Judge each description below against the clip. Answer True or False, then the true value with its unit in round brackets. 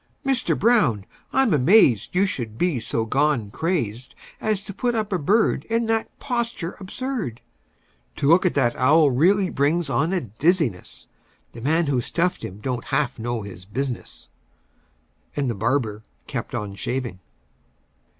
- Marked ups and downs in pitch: True (8.2 semitones)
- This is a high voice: False (145 Hz)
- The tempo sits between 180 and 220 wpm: False (150 wpm)